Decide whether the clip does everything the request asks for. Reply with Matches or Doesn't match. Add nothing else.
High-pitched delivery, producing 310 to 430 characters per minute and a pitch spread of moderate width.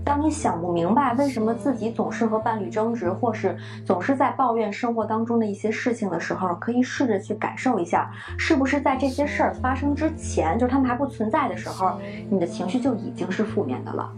Matches